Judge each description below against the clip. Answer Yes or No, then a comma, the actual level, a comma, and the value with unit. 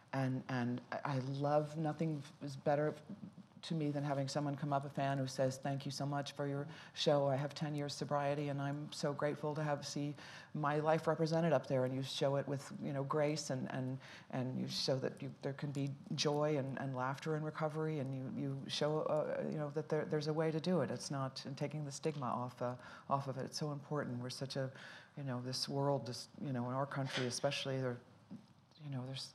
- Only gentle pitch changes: Yes, narrow, 2.2 semitones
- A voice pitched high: No, medium, 140 Hz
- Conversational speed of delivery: No, fast, 230 wpm